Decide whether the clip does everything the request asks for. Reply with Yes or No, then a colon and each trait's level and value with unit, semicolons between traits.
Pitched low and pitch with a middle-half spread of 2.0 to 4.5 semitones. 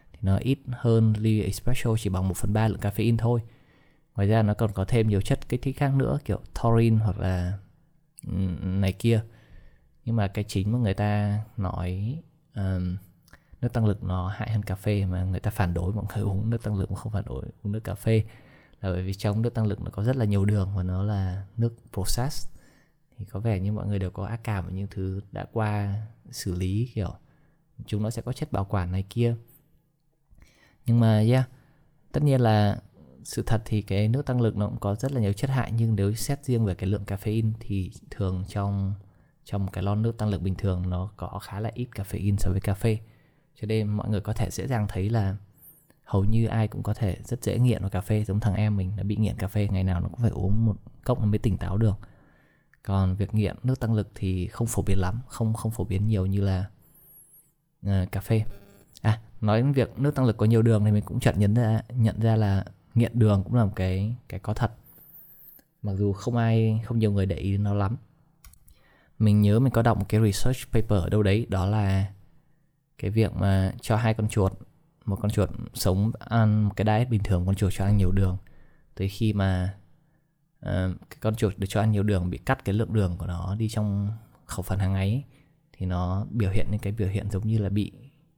Yes: low, 105 Hz; average, 3.1 semitones